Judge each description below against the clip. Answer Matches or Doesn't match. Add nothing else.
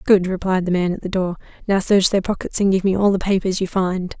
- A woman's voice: Matches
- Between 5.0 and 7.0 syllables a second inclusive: Matches